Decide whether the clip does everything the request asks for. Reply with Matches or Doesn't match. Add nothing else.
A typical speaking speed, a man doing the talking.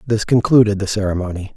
Matches